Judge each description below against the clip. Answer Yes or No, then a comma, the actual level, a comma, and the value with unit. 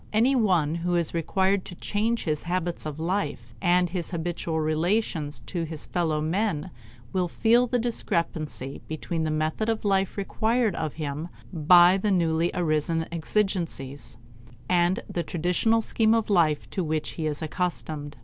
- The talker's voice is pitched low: No, medium, 175 Hz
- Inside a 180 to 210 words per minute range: No, average, 155 wpm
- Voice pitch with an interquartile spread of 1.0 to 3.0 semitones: No, average, 3.8 semitones